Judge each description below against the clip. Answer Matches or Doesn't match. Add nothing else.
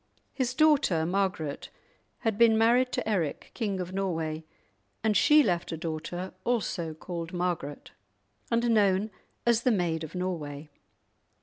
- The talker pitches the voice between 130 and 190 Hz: Matches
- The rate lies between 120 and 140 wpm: Matches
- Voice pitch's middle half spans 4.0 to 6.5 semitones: Matches